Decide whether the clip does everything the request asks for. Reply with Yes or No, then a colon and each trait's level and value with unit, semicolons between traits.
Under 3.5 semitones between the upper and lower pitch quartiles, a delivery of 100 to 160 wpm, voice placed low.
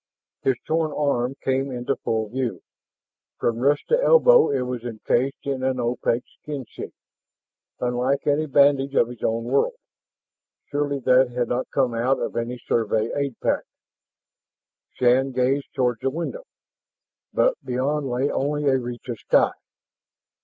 Yes: narrow, 2.6 semitones; average, 145 wpm; low, 130 Hz